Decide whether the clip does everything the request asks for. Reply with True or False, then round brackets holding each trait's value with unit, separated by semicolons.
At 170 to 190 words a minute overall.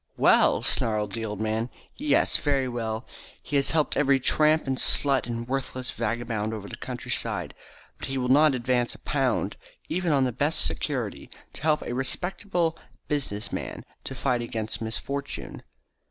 False (160 wpm)